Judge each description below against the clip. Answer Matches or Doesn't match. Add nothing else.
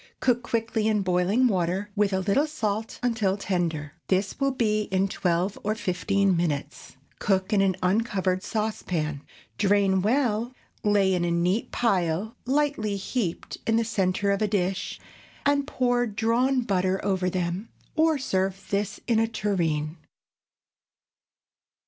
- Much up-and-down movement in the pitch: Doesn't match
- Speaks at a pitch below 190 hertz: Doesn't match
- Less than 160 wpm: Matches